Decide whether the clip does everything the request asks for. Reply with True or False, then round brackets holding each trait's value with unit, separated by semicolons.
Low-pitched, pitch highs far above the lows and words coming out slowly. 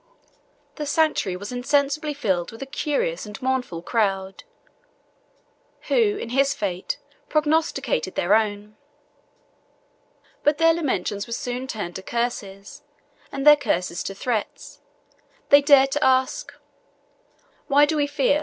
False (255 Hz; 6.3 semitones; 125 wpm)